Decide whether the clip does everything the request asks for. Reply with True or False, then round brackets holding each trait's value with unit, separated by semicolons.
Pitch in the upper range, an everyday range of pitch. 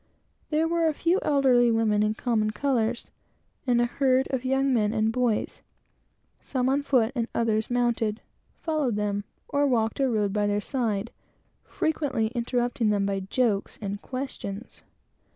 True (240 Hz; 3.8 semitones)